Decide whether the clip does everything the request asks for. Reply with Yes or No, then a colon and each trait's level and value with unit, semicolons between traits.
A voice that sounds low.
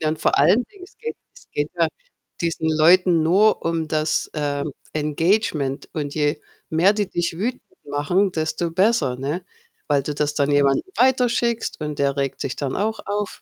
No: medium, 160 Hz